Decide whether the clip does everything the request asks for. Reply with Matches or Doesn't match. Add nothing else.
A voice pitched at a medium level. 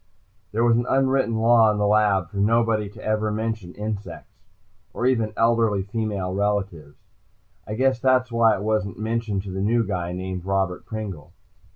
Doesn't match